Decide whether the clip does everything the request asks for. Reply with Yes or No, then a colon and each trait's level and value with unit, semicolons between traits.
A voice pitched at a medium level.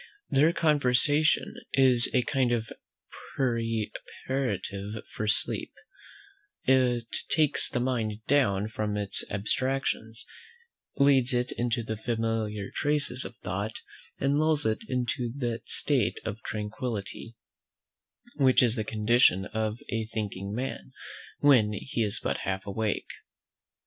No: low, 115 Hz